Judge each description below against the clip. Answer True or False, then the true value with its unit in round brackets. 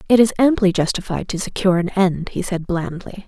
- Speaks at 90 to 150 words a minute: False (200 wpm)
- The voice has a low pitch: False (190 Hz)